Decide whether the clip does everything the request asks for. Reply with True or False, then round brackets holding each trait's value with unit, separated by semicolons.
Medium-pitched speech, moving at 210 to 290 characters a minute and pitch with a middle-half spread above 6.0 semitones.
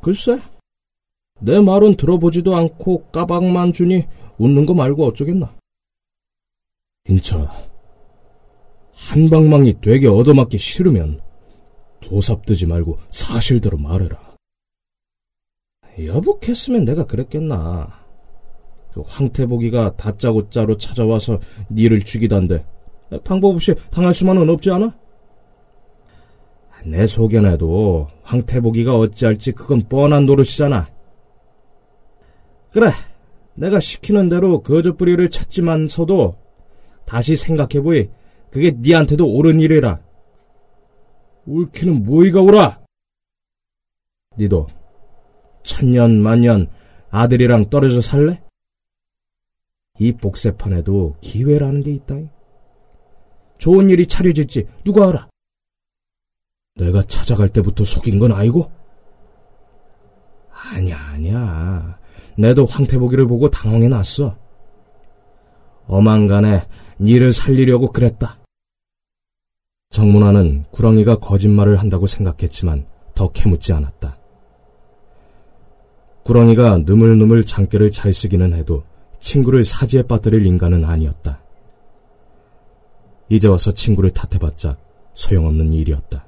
False (110 Hz; 230 characters per minute; 6.7 semitones)